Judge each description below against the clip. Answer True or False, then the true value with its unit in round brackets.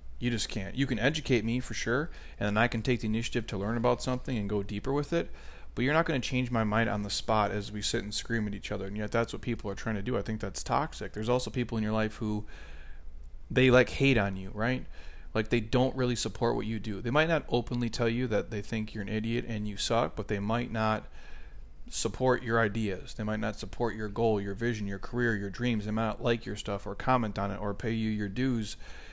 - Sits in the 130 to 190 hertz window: False (110 Hz)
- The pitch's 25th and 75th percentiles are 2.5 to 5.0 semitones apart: True (2.8 semitones)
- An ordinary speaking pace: False (260 wpm)